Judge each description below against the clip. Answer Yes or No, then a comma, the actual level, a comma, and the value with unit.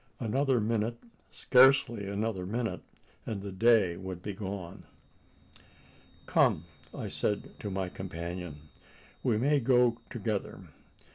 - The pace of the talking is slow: Yes, slow, 115 wpm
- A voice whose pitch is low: Yes, low, 105 Hz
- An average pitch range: Yes, average, 3.9 semitones